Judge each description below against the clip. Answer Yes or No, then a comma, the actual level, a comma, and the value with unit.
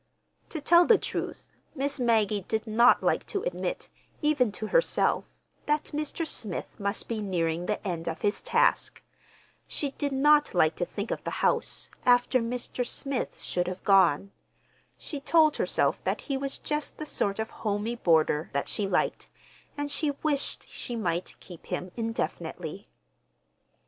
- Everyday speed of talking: Yes, average, 155 wpm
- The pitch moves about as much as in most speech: No, wide, 6.7 semitones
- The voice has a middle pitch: No, high, 230 Hz